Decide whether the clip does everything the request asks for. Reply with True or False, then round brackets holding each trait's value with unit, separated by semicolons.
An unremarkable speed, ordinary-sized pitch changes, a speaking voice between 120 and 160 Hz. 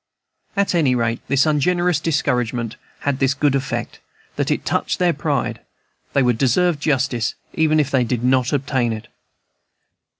True (155 wpm; 3.8 semitones; 135 Hz)